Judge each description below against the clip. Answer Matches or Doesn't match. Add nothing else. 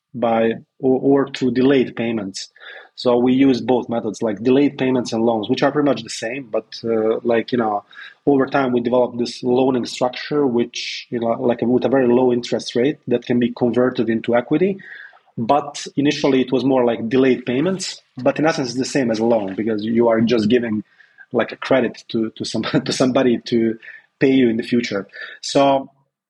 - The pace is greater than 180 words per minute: Matches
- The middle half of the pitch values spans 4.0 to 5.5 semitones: Doesn't match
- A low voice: Matches